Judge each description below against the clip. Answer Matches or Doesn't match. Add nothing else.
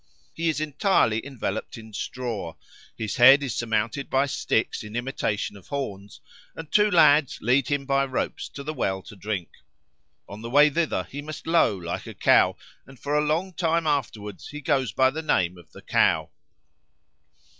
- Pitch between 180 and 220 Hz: Doesn't match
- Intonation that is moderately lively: Doesn't match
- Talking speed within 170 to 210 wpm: Matches